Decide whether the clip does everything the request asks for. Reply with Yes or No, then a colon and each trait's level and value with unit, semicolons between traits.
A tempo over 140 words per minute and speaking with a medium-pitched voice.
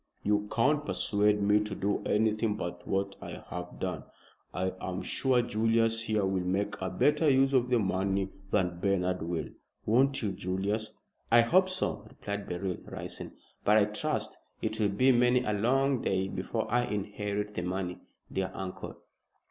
No: average, 165 wpm; low, 105 Hz